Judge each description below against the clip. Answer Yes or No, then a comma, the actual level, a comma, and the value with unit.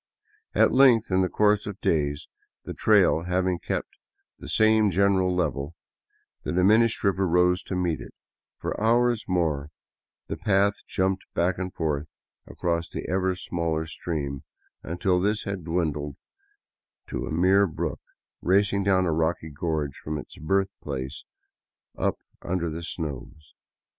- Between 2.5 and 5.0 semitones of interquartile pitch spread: Yes, average, 3.6 semitones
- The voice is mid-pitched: No, very low, 90 Hz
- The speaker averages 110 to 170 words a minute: Yes, average, 145 wpm